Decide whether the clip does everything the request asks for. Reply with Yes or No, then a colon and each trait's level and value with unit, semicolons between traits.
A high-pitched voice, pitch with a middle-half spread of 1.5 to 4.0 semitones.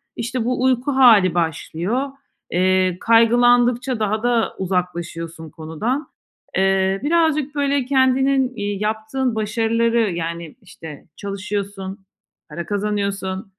No: high, 210 Hz; average, 4.8 semitones